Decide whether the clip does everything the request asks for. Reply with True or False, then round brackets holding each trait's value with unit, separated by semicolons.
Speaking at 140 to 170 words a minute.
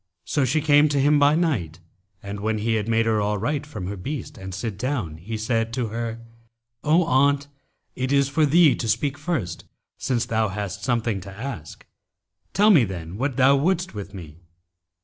False (190 wpm)